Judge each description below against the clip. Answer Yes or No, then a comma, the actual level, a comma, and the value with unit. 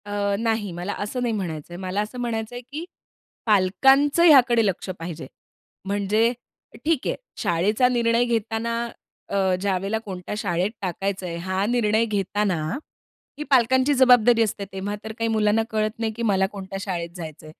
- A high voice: Yes, high, 210 Hz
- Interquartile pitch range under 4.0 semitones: Yes, average, 3.5 semitones